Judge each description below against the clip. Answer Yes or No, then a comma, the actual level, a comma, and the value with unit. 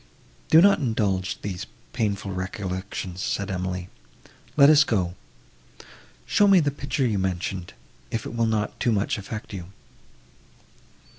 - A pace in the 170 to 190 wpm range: No, slow, 135 wpm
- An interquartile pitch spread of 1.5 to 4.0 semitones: No, average, 4.4 semitones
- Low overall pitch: Yes, low, 100 Hz